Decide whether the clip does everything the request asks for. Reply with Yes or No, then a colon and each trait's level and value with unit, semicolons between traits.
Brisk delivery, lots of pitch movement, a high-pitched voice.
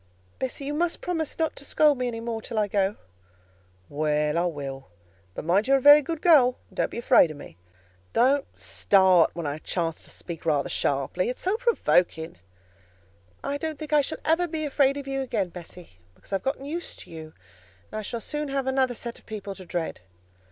Yes: fast, 210 wpm; wide, 8.9 semitones; high, 235 Hz